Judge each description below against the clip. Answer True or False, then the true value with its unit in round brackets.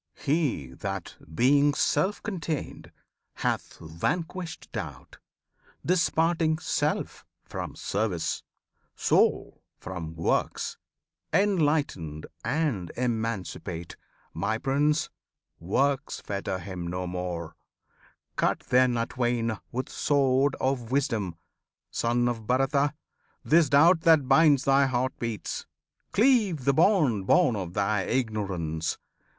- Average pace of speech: False (100 wpm)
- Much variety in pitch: True (7.3 semitones)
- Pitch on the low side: True (125 Hz)